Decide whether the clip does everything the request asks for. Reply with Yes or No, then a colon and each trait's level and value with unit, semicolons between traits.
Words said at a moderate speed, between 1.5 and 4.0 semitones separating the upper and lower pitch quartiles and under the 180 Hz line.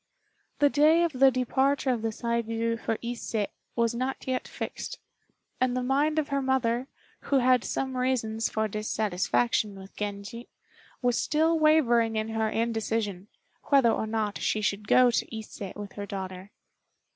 No: average, 155 wpm; average, 3.4 semitones; high, 230 Hz